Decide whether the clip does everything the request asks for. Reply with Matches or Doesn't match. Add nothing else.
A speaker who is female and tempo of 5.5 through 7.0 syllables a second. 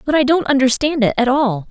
Matches